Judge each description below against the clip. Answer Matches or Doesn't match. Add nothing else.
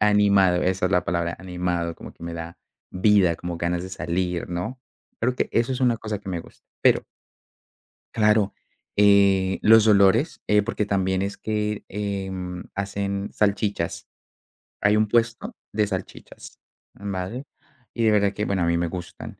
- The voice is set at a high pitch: Doesn't match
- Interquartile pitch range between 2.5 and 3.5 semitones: Matches